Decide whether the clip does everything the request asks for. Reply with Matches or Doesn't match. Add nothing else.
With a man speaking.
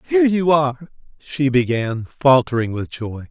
Matches